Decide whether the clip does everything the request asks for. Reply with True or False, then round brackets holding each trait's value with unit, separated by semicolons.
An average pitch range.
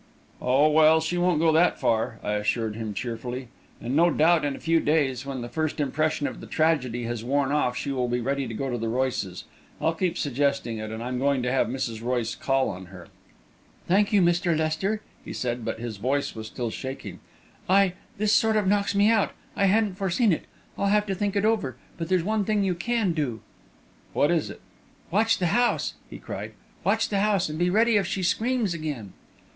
False (7.4 semitones)